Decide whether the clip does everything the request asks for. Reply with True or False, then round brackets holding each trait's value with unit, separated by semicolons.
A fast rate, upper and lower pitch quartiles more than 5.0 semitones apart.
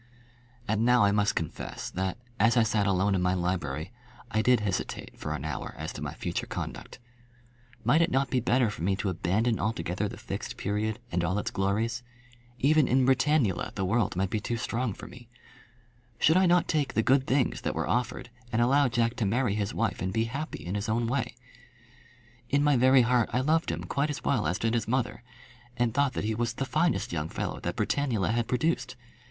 False (210 wpm; 4.4 semitones)